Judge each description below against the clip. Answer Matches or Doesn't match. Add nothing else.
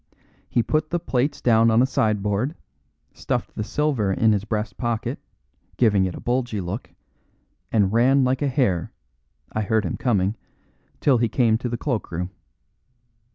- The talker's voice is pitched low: Matches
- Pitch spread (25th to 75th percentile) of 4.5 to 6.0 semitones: Doesn't match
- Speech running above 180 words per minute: Doesn't match